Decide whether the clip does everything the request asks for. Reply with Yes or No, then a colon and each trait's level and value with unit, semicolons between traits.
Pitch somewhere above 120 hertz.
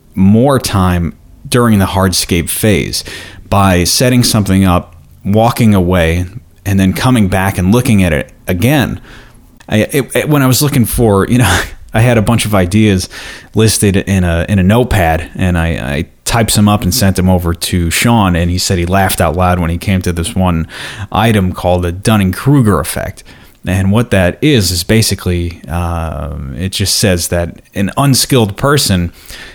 No: very low, 95 Hz